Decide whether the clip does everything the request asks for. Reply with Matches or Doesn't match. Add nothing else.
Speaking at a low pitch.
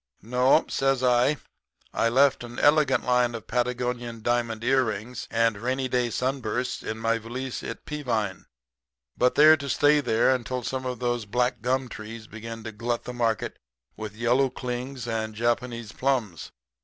Matches